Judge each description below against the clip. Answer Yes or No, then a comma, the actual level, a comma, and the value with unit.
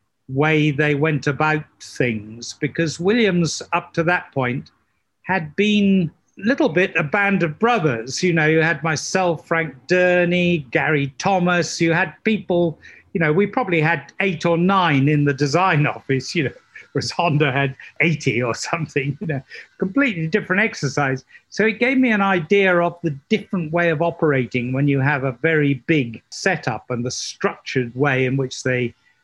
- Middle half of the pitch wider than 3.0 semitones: Yes, average, 4.4 semitones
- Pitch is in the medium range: Yes, medium, 160 Hz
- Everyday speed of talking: Yes, average, 170 wpm